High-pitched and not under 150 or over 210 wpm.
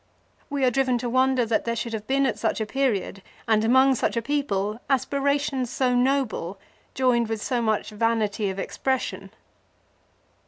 Yes: high, 245 Hz; average, 165 wpm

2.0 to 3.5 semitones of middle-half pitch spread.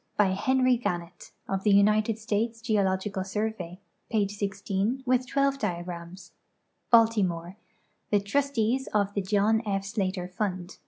Yes: average, 3.0 semitones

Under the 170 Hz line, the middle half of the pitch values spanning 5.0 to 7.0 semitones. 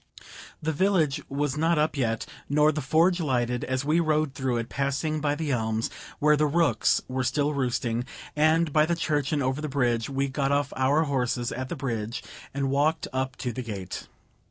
No: medium, 140 Hz; average, 3.2 semitones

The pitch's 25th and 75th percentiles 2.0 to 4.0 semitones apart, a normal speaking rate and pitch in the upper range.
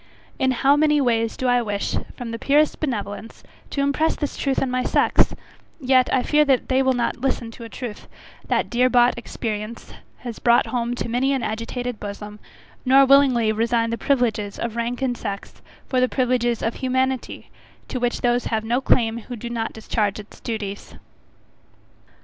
Yes: narrow, 2.4 semitones; average, 180 wpm; high, 245 Hz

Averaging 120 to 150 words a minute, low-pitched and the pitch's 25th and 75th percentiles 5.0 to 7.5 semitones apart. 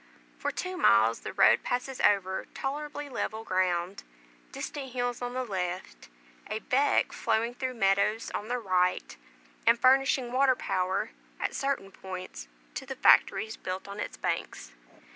No: average, 145 wpm; high, 220 Hz; wide, 5.5 semitones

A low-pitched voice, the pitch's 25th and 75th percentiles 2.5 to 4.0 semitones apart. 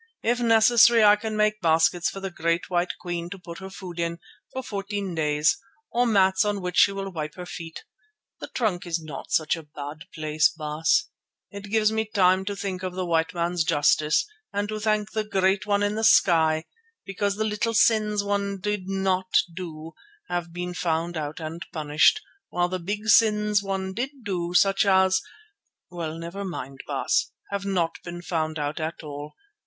No: medium, 185 Hz; average, 3.7 semitones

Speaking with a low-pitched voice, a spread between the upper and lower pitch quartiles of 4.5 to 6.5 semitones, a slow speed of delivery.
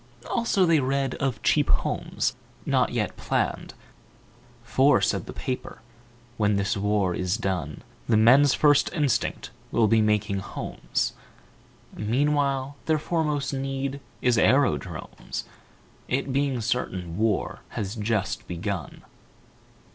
Yes: low, 120 Hz; average, 5.2 semitones; slow, 115 wpm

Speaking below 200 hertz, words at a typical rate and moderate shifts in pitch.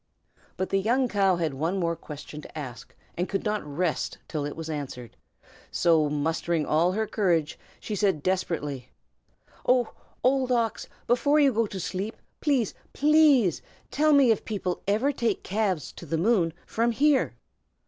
No: high, 190 Hz; average, 160 wpm; wide, 6.6 semitones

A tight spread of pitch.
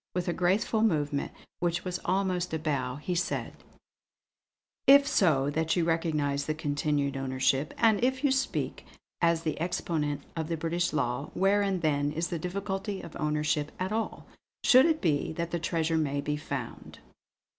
No: average, 3.8 semitones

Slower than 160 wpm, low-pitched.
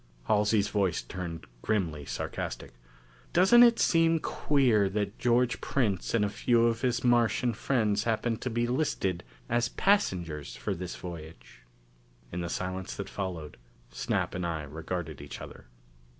Yes: average, 145 wpm; low, 105 Hz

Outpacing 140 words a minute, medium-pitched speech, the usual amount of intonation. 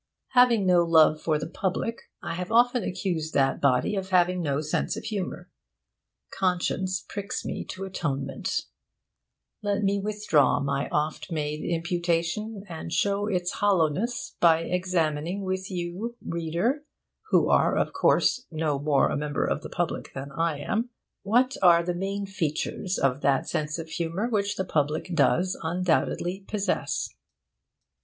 Yes: average, 150 wpm; medium, 180 Hz; average, 4.1 semitones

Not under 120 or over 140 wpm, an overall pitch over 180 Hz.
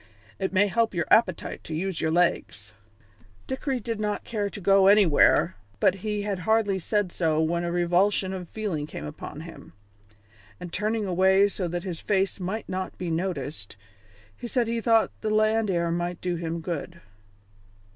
No: average, 175 wpm; high, 190 Hz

